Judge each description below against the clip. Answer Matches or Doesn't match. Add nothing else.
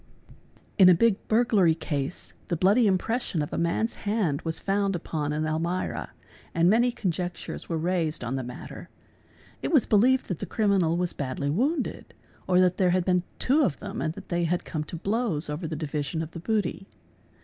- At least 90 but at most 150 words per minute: Doesn't match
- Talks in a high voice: Doesn't match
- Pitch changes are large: Doesn't match